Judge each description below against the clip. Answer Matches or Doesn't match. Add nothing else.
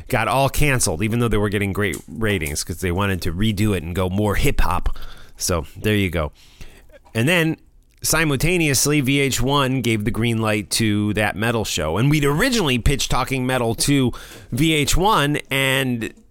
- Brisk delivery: Doesn't match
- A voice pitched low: Matches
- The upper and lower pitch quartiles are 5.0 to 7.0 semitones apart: Matches